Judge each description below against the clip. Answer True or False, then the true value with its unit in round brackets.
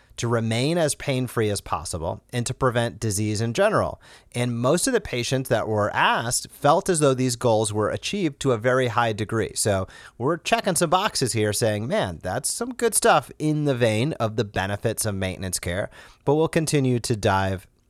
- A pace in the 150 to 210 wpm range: True (200 wpm)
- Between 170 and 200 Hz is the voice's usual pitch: False (120 Hz)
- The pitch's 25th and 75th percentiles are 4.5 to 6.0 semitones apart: True (4.8 semitones)